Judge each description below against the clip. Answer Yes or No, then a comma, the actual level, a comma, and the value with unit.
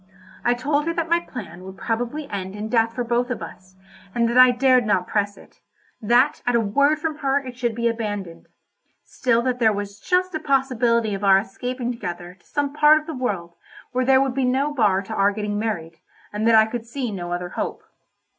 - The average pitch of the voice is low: No, high, 235 Hz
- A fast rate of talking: Yes, fast, 215 wpm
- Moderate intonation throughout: Yes, average, 4.4 semitones